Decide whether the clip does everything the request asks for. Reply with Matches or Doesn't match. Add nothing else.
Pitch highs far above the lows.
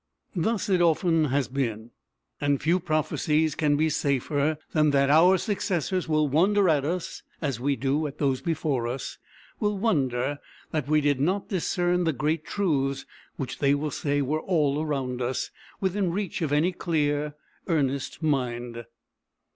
Doesn't match